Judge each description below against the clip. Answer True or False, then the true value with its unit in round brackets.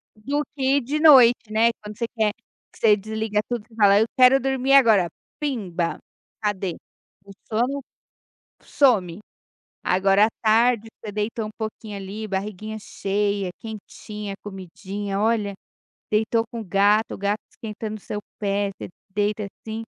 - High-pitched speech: True (215 Hz)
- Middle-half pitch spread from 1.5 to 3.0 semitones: True (2.4 semitones)